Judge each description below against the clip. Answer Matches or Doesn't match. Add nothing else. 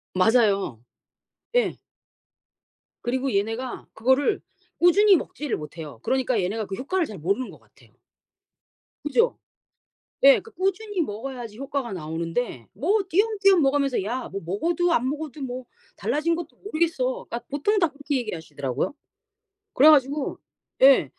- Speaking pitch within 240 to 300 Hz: Matches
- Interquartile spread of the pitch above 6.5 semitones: Matches